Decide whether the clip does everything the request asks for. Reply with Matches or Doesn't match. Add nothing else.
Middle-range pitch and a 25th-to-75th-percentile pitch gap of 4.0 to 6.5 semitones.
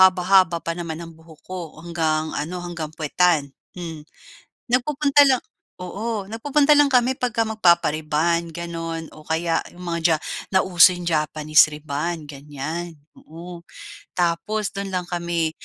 Doesn't match